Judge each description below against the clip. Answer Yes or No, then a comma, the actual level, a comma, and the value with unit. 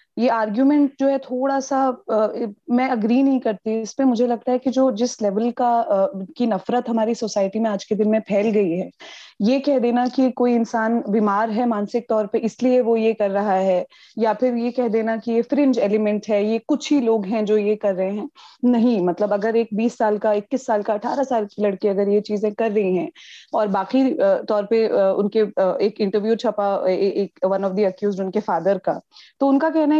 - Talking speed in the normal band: No, fast, 225 wpm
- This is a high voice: Yes, high, 225 Hz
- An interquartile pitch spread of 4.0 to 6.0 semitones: No, average, 3.3 semitones